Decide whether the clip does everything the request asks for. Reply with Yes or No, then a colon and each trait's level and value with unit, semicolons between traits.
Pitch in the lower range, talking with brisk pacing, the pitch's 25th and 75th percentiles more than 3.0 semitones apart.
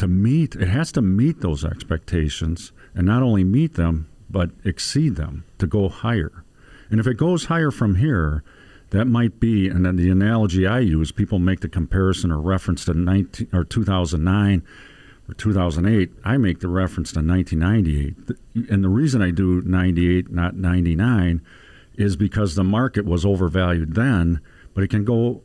No: very low, 95 Hz; average, 170 wpm; average, 3.8 semitones